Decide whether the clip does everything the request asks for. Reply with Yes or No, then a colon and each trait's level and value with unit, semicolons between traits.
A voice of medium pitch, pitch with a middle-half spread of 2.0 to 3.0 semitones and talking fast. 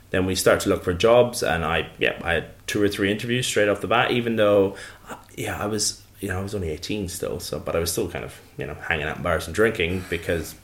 No: low, 100 Hz; narrow, 2.6 semitones; fast, 270 wpm